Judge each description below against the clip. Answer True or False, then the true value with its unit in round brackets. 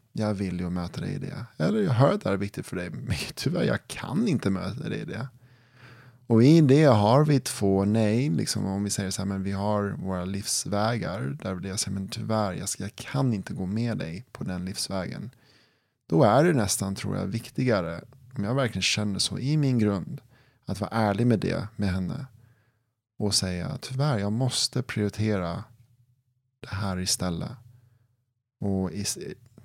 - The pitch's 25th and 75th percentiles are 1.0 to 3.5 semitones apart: False (4.2 semitones)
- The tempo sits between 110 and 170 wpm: False (190 wpm)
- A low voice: True (110 Hz)